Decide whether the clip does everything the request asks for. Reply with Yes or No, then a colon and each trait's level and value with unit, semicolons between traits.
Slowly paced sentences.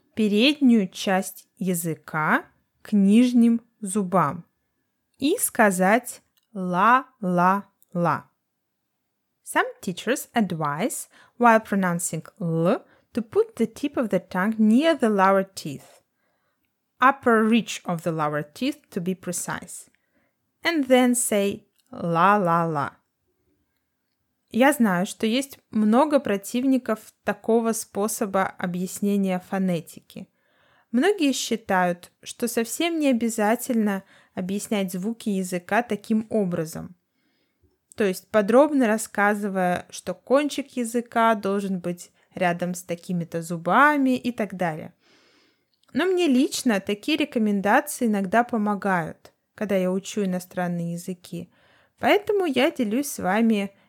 Yes: slow, 105 wpm